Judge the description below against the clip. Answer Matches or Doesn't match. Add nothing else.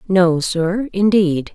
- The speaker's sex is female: Matches